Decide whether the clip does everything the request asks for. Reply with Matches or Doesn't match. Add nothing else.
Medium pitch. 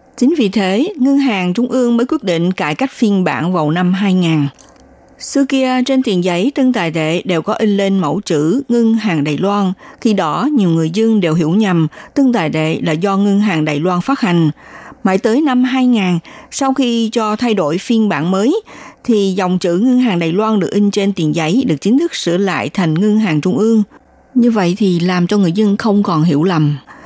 Doesn't match